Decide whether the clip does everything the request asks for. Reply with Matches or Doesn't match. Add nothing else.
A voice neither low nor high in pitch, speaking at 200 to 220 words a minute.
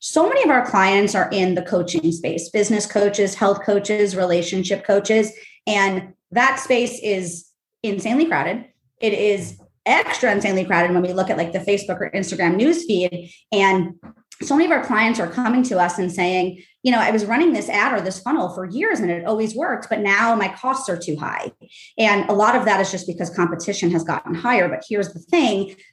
Doesn't match